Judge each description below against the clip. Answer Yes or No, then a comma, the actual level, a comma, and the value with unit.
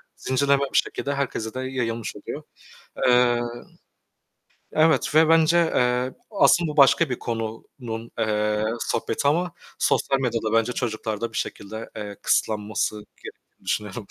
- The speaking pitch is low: Yes, low, 120 Hz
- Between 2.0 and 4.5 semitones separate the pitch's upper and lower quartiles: Yes, average, 4.2 semitones